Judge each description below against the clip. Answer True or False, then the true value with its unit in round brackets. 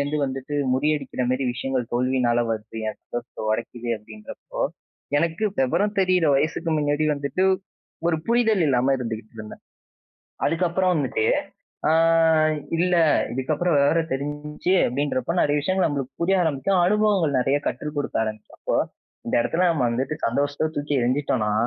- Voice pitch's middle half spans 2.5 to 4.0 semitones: False (4.7 semitones)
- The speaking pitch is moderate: True (145 Hz)